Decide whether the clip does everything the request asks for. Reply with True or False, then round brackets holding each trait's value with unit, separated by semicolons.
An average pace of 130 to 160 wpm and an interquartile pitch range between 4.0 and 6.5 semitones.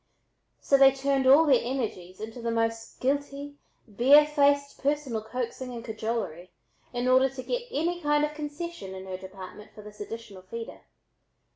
True (155 wpm; 4.6 semitones)